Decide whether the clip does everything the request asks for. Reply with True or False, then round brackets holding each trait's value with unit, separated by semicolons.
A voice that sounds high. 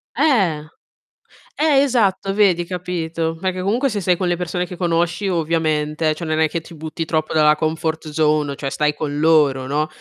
False (165 Hz)